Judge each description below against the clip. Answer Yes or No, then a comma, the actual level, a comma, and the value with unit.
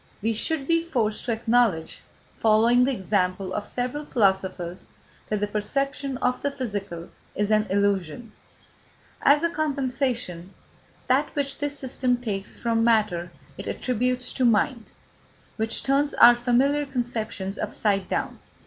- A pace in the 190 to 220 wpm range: No, slow, 135 wpm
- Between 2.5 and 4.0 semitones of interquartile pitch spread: No, average, 4.5 semitones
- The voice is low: No, high, 235 Hz